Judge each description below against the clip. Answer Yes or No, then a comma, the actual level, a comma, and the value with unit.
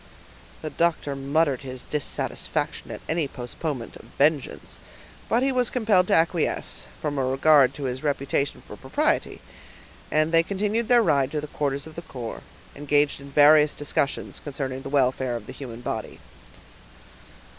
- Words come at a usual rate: Yes, average, 155 wpm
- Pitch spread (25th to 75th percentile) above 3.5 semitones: No, average, 3.1 semitones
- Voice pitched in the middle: Yes, medium, 145 Hz